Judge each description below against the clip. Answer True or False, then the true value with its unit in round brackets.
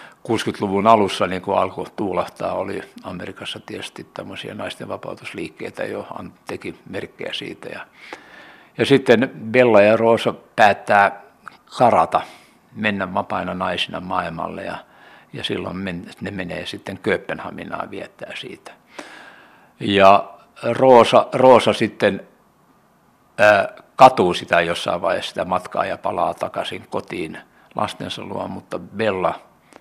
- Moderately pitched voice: False (100 Hz)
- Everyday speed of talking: True (115 wpm)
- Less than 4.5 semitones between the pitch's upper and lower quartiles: True (3.0 semitones)